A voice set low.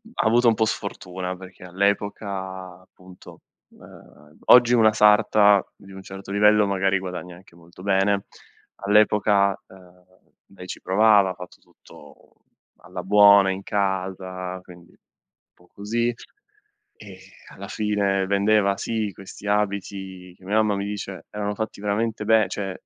Yes: low, 100 Hz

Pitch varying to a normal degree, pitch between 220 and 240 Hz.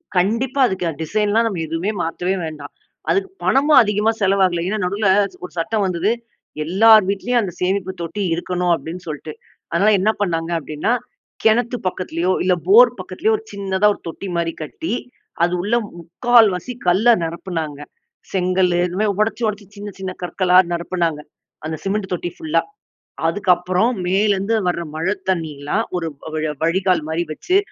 No: average, 3.9 semitones; medium, 185 Hz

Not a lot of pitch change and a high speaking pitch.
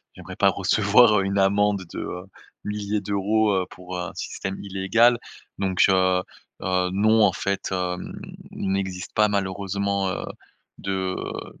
No: narrow, 1.7 semitones; very low, 95 Hz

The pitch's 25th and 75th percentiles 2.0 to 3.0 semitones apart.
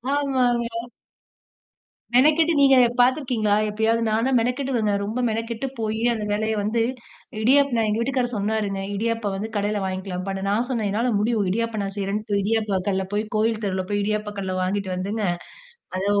Yes: average, 2.7 semitones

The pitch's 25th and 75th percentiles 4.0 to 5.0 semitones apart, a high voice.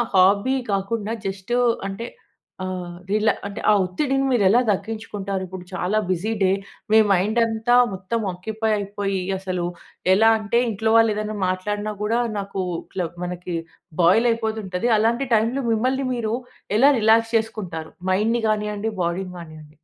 No: average, 3.1 semitones; high, 210 Hz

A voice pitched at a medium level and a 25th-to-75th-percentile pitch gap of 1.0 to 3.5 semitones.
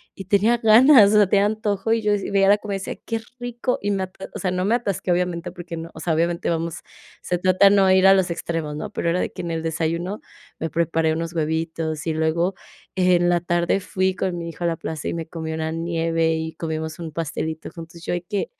Yes: medium, 175 Hz; average, 3.2 semitones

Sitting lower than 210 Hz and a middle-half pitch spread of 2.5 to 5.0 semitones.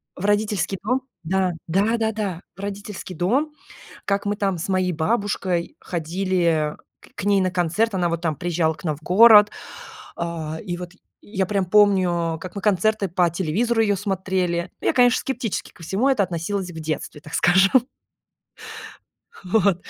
Yes: high, 190 Hz; average, 3.2 semitones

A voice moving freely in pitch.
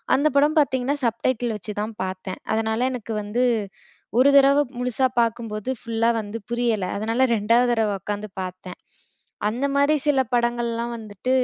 No: average, 3.1 semitones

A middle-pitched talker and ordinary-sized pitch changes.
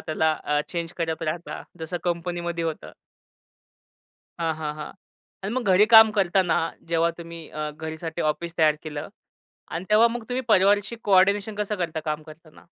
Yes: medium, 170 Hz; average, 3.7 semitones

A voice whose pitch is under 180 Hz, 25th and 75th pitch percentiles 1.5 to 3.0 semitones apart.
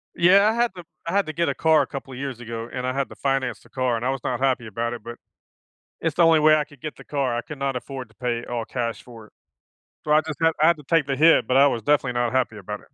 No: low, 135 Hz; average, 4.3 semitones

